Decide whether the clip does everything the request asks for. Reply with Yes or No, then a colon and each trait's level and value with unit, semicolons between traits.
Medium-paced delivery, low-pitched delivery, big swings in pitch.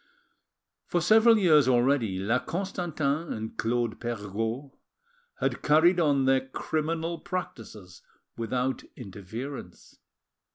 No: slow, 95 wpm; low, 130 Hz; wide, 6.3 semitones